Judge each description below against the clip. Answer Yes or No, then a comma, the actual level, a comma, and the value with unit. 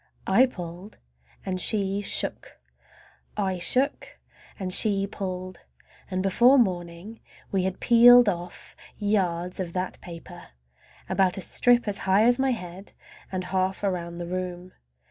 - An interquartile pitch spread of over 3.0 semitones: No, narrow, 2.5 semitones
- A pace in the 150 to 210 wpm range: No, slow, 135 wpm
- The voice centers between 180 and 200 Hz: Yes, high, 190 Hz